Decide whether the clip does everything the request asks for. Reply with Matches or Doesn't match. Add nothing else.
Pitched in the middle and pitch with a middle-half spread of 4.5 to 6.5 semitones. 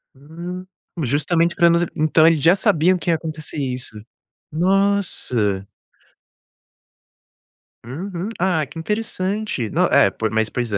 Matches